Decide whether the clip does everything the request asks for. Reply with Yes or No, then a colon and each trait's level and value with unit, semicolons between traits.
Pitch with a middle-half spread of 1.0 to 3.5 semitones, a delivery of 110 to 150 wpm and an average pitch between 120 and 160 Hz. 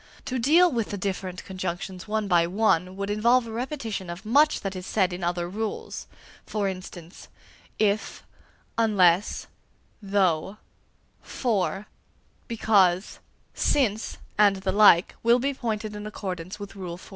No: average, 3.2 semitones; average, 140 wpm; high, 200 Hz